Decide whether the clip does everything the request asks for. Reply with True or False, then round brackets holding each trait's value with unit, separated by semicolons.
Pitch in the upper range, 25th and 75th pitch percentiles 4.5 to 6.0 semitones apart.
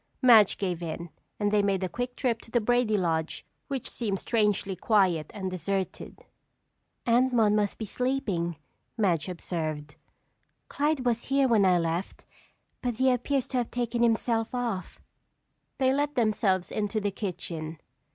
True (210 Hz; 4.9 semitones)